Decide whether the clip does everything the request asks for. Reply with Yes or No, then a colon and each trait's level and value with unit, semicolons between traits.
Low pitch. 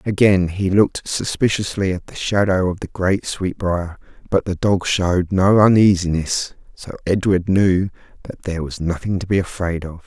Yes: very low, 95 Hz